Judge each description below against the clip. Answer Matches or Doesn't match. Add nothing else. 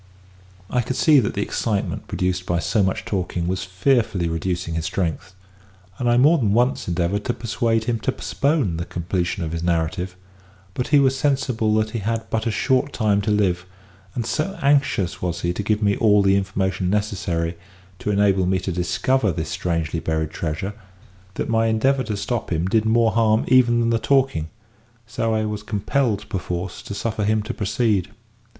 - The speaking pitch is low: Matches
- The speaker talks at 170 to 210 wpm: Matches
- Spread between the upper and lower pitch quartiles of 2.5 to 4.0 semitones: Doesn't match